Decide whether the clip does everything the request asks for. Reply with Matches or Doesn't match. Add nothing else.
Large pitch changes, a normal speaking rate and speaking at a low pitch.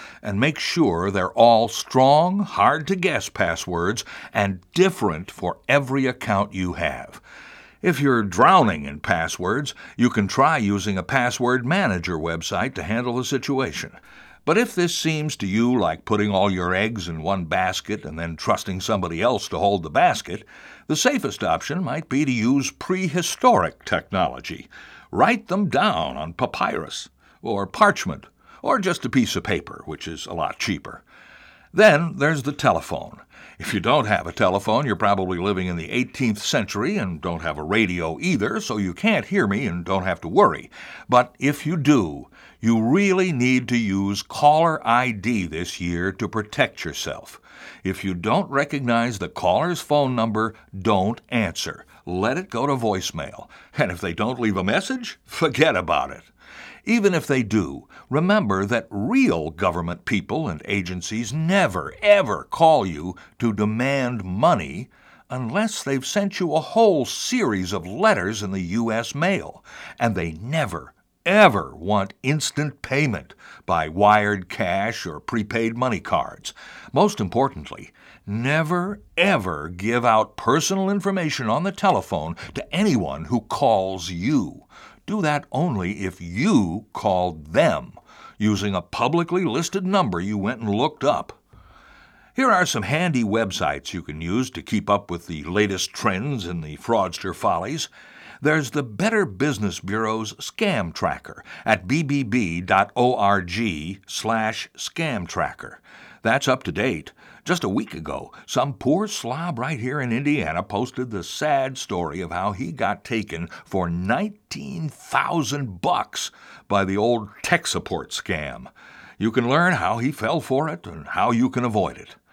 Matches